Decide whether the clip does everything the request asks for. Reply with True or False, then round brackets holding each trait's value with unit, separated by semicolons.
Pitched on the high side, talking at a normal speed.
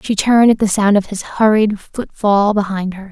False (205 Hz; 230 wpm)